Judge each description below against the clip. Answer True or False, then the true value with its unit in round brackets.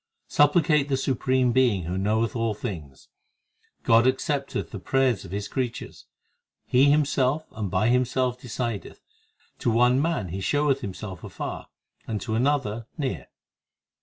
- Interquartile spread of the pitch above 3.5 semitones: True (4.2 semitones)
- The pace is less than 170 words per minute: True (140 wpm)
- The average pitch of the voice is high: False (125 Hz)